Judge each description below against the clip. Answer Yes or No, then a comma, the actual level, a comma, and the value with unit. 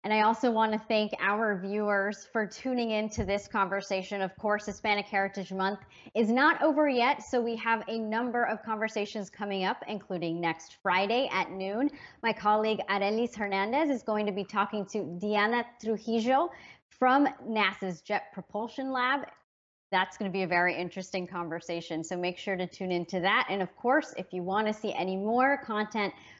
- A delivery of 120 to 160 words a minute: No, average, 180 wpm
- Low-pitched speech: No, high, 210 Hz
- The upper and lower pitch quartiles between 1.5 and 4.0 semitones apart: Yes, average, 3.0 semitones